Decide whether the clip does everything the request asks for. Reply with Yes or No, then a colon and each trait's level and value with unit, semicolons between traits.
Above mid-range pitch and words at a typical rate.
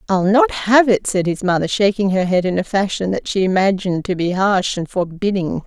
No: high, 195 Hz; fast, 220 wpm